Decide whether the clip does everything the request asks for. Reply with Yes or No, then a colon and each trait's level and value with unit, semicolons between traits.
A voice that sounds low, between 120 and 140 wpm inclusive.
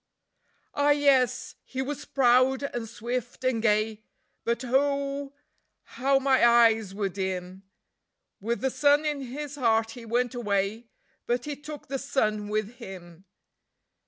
No: high, 245 Hz; slow, 135 wpm